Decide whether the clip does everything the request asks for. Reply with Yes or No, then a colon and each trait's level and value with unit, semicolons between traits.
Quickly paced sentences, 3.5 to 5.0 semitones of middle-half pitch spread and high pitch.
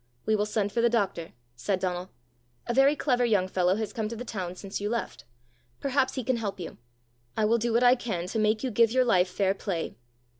Yes: fast, 230 wpm; average, 3.9 semitones; high, 215 Hz